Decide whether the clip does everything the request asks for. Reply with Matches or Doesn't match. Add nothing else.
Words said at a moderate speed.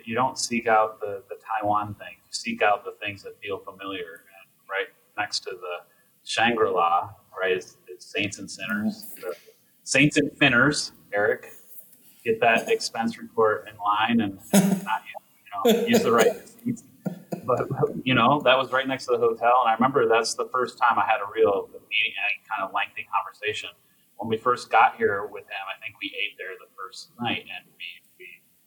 Matches